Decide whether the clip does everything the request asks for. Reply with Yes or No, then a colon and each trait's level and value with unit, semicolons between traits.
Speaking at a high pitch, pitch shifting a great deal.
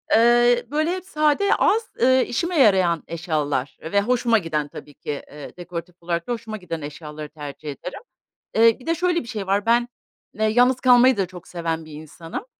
Yes: high, 200 Hz; wide, 7.1 semitones